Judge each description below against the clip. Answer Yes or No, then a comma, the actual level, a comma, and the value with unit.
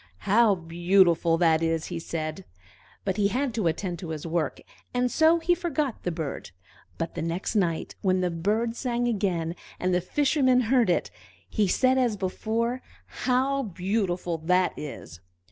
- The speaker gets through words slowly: No, average, 160 wpm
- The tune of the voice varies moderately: No, wide, 6.1 semitones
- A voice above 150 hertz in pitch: Yes, high, 190 Hz